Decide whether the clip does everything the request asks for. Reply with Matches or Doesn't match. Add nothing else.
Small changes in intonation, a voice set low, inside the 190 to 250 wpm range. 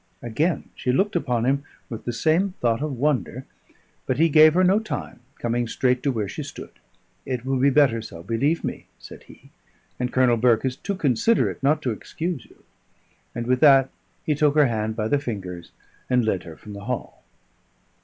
Doesn't match